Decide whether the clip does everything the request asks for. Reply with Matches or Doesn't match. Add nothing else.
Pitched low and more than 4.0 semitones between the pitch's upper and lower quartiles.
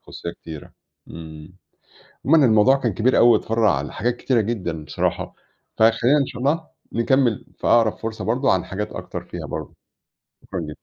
Matches